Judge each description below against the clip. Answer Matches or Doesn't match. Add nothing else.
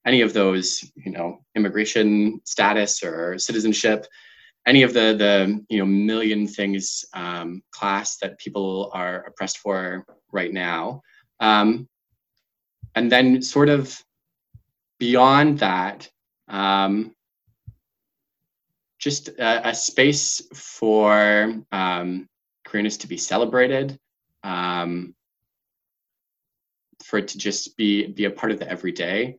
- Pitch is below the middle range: Matches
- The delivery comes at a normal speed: Doesn't match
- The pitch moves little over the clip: Doesn't match